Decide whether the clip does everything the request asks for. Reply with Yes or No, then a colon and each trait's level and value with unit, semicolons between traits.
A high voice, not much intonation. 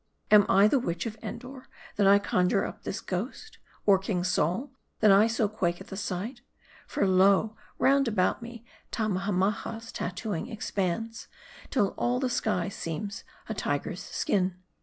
No: high, 205 Hz; average, 3.5 semitones